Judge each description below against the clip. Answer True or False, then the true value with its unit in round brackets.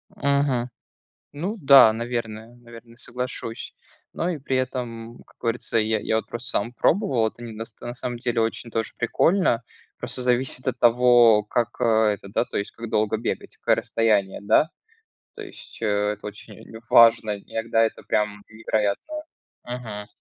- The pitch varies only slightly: True (2.0 semitones)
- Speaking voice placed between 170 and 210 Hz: False (115 Hz)